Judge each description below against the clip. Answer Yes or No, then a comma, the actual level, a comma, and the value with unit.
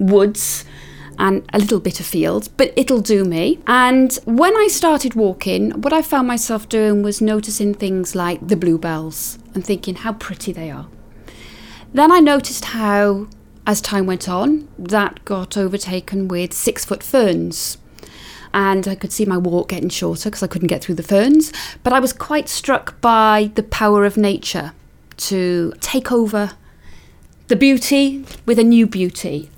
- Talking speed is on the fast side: No, average, 165 wpm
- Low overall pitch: No, high, 205 Hz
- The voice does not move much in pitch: No, average, 4.8 semitones